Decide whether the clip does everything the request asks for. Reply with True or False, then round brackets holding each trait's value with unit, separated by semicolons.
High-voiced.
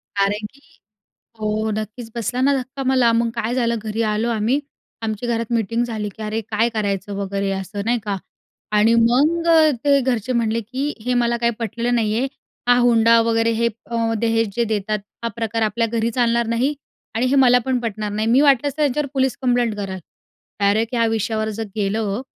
True (230 Hz)